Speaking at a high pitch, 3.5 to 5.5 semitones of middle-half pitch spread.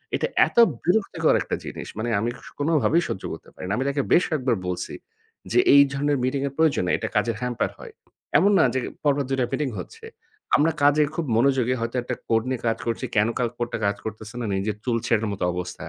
No: low, 130 Hz; average, 4.4 semitones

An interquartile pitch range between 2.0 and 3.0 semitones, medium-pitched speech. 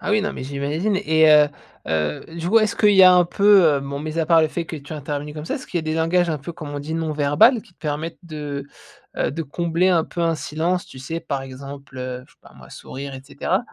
No: average, 3.5 semitones; medium, 155 Hz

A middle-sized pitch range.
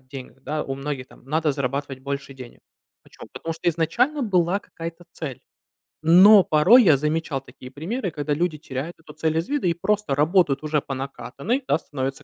Yes: average, 4.0 semitones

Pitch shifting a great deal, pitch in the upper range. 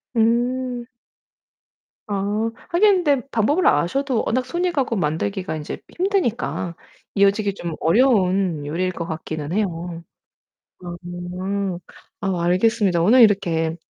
Yes: wide, 6.0 semitones; high, 195 Hz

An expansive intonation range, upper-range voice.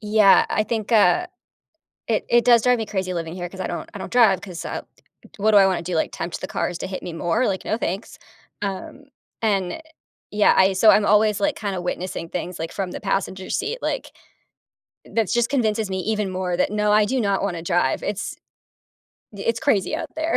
No: average, 3.2 semitones; high, 200 Hz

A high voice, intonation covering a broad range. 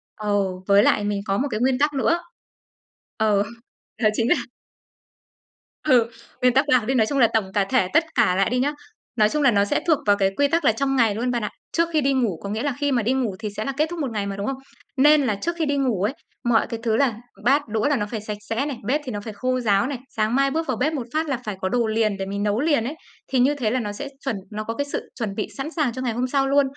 No: high, 245 Hz; average, 4.7 semitones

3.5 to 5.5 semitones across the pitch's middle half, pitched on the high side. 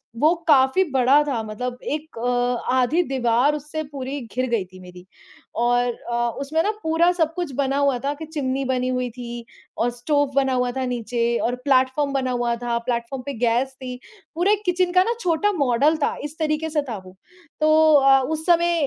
Yes: average, 4.1 semitones; very high, 265 Hz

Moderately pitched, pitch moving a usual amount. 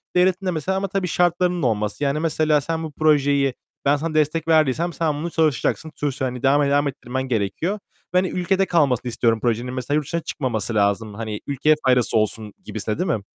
Yes: medium, 145 Hz; average, 4.9 semitones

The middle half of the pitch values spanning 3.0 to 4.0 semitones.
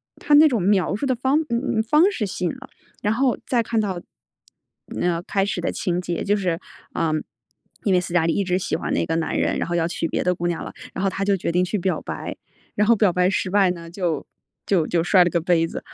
Yes: average, 3.4 semitones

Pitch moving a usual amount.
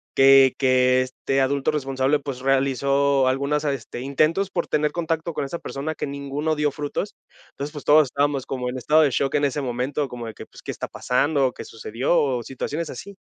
No: narrow, 2.2 semitones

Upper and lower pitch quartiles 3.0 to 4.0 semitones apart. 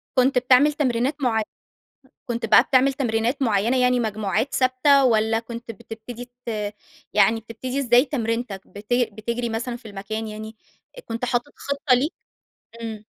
No: narrow, 2.6 semitones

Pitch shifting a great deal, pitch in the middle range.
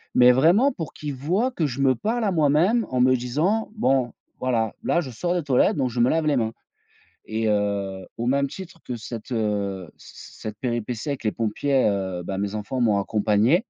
No: wide, 6.0 semitones; low, 125 Hz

